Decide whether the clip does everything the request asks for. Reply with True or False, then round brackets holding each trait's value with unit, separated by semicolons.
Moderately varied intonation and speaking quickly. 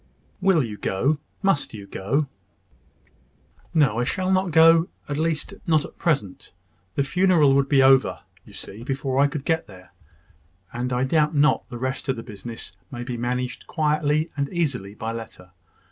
False (4.4 semitones; 170 wpm)